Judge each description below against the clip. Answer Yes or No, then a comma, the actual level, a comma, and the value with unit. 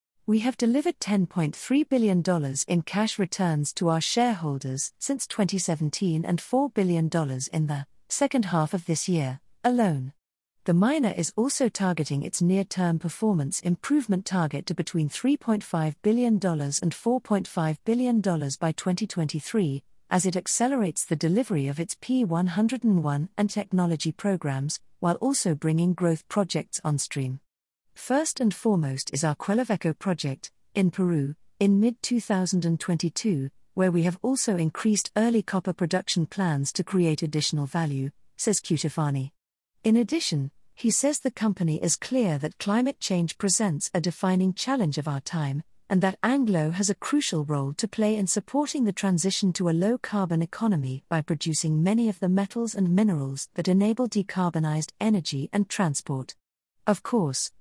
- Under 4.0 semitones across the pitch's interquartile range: No, average, 5.3 semitones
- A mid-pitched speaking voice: Yes, medium, 180 Hz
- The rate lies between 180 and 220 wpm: No, average, 145 wpm